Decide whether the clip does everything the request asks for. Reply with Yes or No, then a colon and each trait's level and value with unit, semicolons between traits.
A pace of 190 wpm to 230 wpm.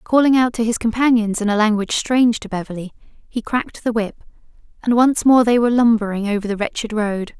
Yes: fast, 205 wpm